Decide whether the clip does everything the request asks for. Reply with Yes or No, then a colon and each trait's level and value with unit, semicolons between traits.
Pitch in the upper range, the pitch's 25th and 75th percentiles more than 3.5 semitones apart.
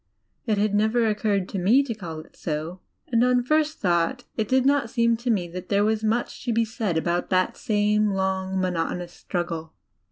Yes: high, 210 Hz; average, 4.3 semitones